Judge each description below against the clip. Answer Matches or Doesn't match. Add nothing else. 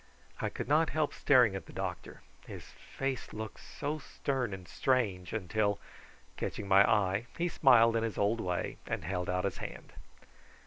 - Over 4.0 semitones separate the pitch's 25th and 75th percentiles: Matches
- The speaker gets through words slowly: Doesn't match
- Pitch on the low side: Matches